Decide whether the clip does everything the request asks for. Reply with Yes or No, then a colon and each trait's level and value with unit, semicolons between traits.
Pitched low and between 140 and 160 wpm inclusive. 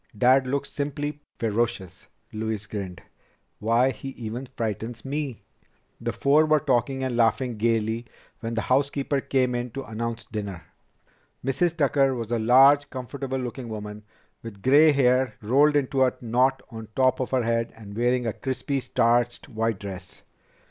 Yes: low, 125 Hz; average, 155 wpm